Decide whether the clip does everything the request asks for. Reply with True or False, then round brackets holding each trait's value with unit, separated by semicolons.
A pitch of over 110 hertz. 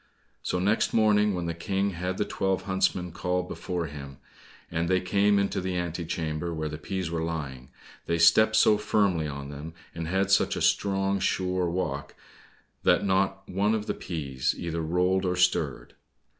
False (90 Hz)